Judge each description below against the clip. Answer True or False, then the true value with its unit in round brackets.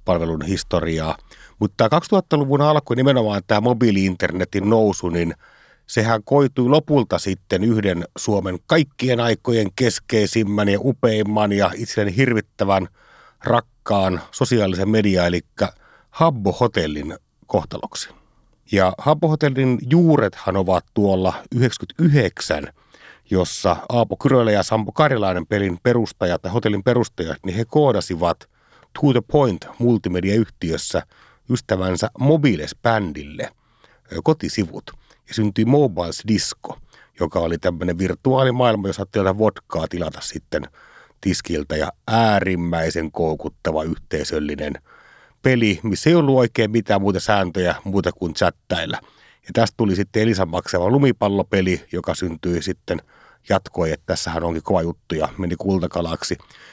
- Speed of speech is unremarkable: True (115 wpm)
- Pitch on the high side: False (105 Hz)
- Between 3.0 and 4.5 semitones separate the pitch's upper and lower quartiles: False (4.9 semitones)